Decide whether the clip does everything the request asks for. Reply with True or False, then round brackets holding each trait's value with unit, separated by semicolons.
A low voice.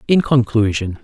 True (120 Hz)